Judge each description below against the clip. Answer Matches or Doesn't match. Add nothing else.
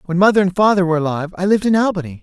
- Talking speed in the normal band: Doesn't match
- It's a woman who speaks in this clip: Doesn't match